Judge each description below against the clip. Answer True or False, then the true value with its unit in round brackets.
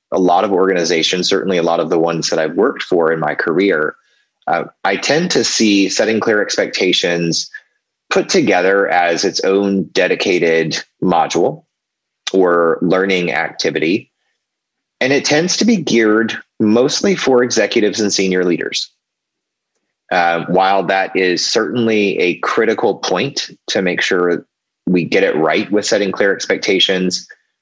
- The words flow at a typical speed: True (145 wpm)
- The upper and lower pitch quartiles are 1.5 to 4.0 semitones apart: True (3.4 semitones)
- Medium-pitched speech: False (95 Hz)